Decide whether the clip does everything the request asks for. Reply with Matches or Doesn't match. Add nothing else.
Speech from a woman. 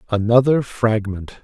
Doesn't match